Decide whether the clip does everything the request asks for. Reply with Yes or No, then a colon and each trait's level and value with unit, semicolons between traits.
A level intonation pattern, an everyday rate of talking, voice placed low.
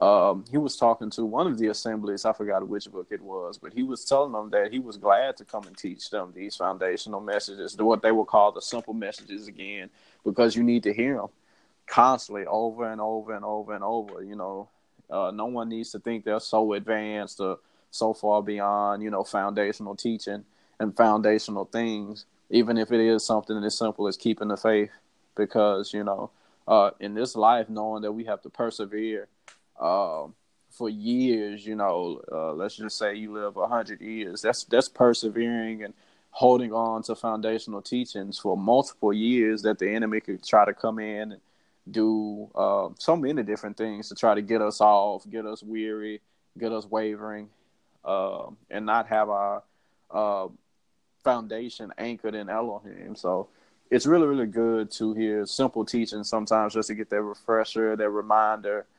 Yes: narrow, 1.3 semitones; average, 185 wpm; low, 110 Hz